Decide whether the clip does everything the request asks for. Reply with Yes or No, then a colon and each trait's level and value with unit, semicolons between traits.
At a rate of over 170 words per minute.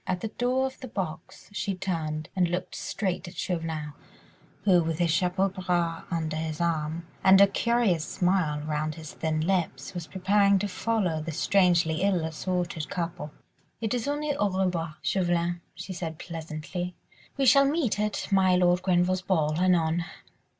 No: average, 165 wpm